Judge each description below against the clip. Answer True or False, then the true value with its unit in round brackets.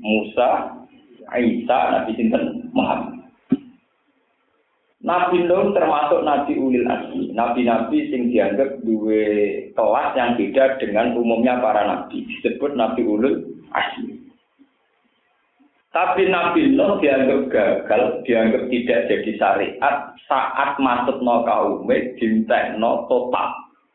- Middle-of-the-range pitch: True (150 Hz)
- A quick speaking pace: False (105 wpm)